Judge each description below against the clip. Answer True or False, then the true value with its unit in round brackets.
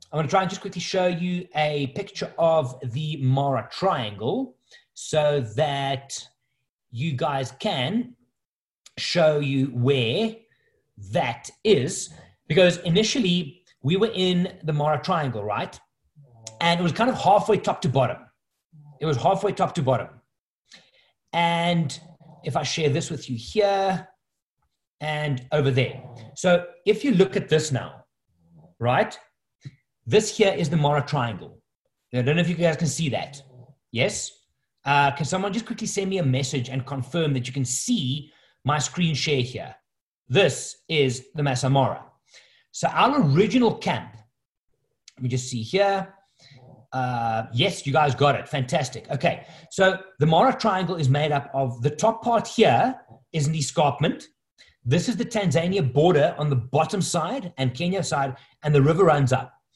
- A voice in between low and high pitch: True (150 Hz)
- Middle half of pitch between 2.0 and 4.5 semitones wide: False (5.6 semitones)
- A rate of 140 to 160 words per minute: True (155 wpm)